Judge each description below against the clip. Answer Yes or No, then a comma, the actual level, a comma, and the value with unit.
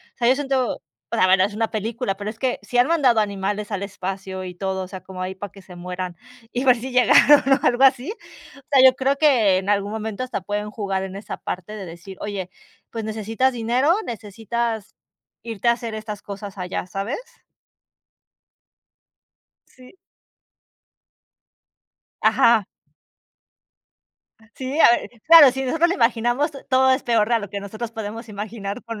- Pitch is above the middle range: Yes, high, 220 Hz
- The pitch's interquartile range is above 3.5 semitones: Yes, average, 4.1 semitones